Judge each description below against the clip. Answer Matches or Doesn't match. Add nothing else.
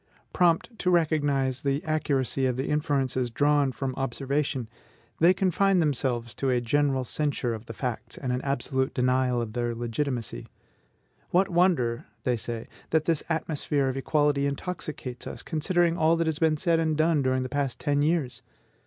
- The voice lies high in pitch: Doesn't match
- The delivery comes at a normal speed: Matches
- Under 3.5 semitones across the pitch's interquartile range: Doesn't match